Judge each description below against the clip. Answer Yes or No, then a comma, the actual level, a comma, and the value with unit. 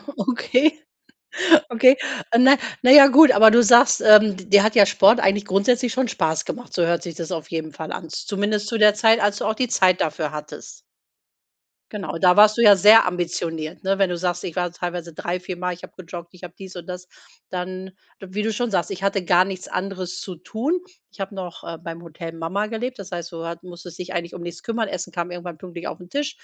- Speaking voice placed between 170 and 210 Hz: Yes, medium, 185 Hz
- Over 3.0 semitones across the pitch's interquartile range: Yes, average, 3.8 semitones